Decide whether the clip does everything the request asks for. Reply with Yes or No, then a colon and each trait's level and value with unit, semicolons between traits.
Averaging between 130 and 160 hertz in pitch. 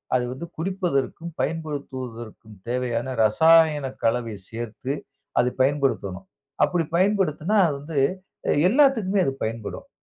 Yes: medium, 140 Hz